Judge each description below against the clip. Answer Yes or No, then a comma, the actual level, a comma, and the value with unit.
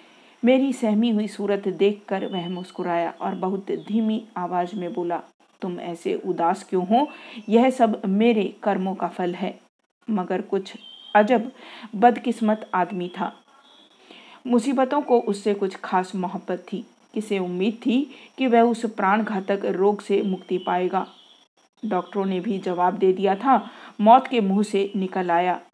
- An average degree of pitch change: Yes, average, 4.0 semitones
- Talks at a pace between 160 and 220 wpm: No, average, 150 wpm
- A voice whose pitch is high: Yes, high, 200 Hz